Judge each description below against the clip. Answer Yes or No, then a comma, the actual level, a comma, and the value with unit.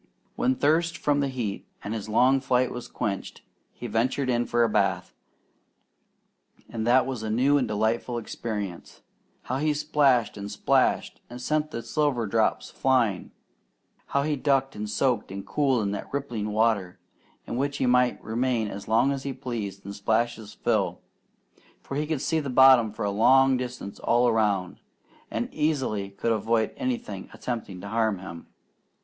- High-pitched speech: No, low, 120 Hz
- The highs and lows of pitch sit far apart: No, average, 3.9 semitones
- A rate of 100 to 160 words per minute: No, average, 170 wpm